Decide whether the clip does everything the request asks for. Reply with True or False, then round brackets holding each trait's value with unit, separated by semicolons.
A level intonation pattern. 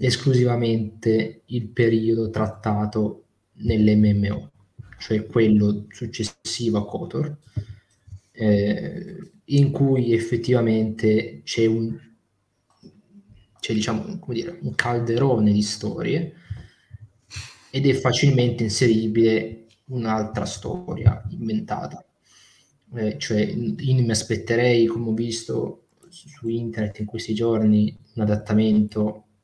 True (2.1 semitones)